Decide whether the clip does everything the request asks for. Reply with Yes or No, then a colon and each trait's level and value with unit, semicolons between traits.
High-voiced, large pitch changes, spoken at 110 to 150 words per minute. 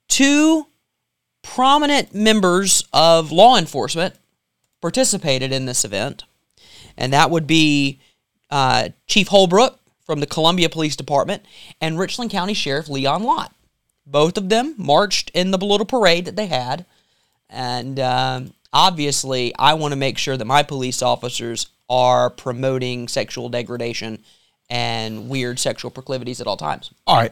No: medium, 140 Hz; wide, 6.4 semitones; average, 140 wpm